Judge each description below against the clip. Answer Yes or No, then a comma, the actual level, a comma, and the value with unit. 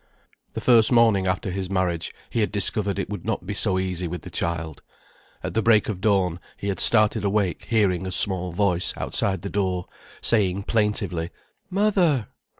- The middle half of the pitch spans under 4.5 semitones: Yes, average, 2.8 semitones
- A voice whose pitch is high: No, low, 100 Hz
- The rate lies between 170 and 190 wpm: Yes, average, 175 wpm